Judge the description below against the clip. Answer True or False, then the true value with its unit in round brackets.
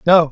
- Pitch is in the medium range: True (160 Hz)